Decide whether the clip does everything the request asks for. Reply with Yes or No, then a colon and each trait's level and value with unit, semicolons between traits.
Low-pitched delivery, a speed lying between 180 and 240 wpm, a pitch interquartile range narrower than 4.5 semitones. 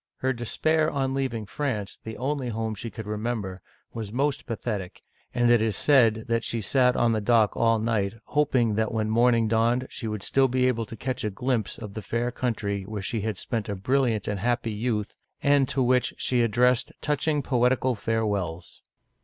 Yes: low, 115 Hz; average, 185 wpm; average, 2.9 semitones